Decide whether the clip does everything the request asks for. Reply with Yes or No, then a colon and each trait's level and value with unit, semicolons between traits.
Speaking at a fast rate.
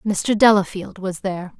No: average, 150 wpm